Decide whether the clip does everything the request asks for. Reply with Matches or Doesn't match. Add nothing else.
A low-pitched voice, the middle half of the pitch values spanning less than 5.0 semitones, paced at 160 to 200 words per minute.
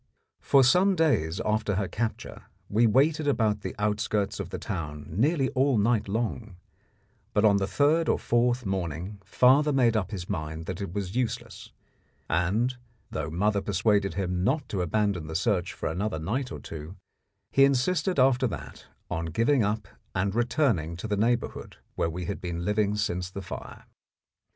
Doesn't match